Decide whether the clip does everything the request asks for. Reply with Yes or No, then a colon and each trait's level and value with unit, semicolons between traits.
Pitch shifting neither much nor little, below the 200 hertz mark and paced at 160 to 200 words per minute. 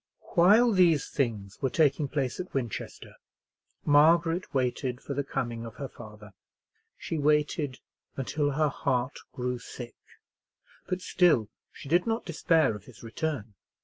No: average, 4.9 semitones; medium, 140 Hz; average, 140 wpm